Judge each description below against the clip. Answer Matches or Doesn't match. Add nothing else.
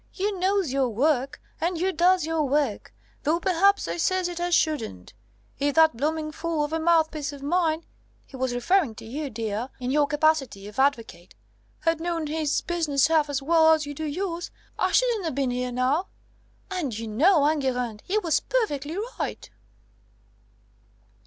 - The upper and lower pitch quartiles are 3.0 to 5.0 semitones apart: Matches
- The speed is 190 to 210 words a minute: Doesn't match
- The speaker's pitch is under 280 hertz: Doesn't match